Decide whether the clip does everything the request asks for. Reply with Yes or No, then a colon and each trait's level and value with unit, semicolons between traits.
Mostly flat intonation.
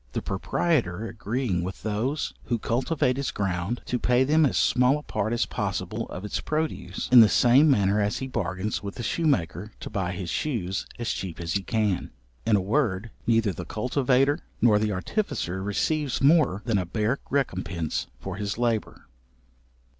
No: average, 5.3 semitones